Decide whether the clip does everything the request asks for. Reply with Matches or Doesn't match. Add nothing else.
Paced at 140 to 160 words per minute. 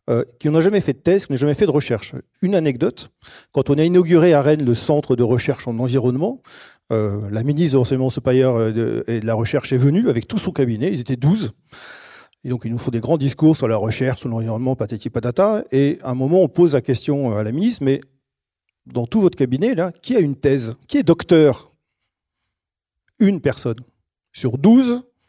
Doesn't match